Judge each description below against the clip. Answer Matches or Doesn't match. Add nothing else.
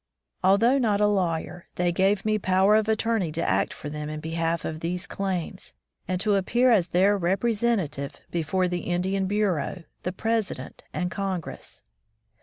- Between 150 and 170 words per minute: Matches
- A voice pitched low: Doesn't match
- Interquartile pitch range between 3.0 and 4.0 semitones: Matches